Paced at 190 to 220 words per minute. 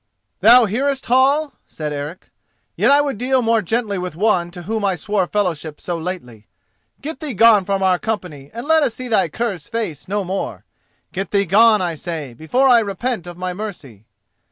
Yes: average, 195 wpm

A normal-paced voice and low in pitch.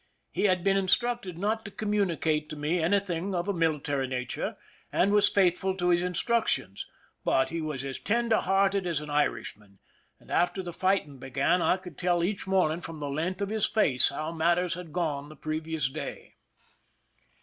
No: average, 180 wpm; medium, 175 Hz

